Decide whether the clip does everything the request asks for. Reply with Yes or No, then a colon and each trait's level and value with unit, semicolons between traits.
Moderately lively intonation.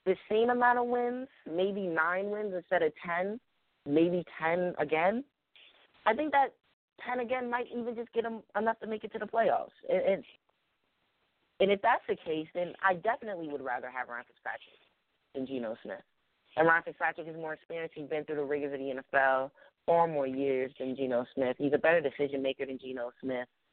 No: wide, 7.9 semitones